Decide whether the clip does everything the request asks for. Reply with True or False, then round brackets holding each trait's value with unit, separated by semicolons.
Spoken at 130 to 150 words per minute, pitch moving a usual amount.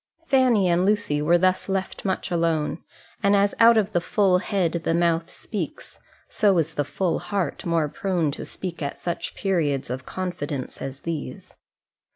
False (170 wpm; 3.7 semitones)